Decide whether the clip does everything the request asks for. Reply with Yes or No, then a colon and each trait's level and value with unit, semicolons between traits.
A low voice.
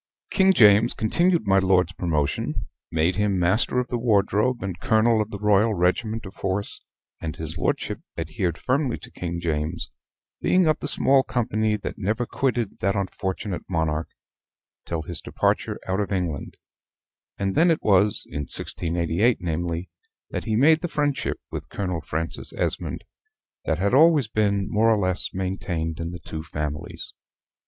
Yes: low, 100 Hz